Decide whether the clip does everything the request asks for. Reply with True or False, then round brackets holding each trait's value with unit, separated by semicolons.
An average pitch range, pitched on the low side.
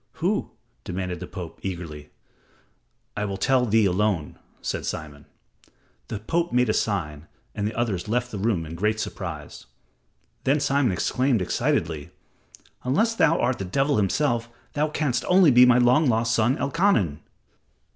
False (6.2 semitones; 110 Hz)